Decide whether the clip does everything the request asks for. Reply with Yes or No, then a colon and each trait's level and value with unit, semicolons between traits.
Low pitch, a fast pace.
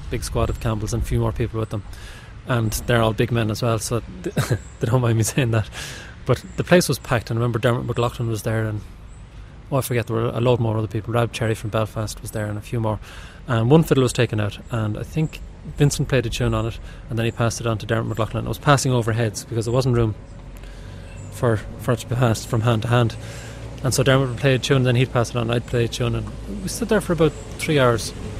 Yes: low, 115 Hz; fast, 265 wpm